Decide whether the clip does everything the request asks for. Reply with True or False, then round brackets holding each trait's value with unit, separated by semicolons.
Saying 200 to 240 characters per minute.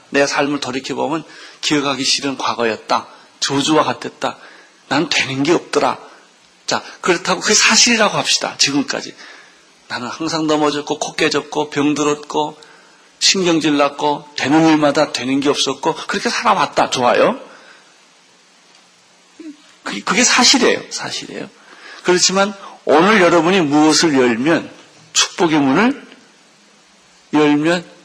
False (270 characters per minute)